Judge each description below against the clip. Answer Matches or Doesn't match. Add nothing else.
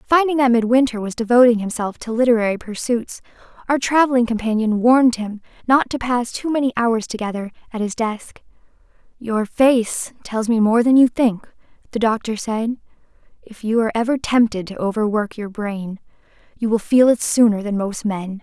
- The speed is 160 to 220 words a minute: Matches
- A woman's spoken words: Matches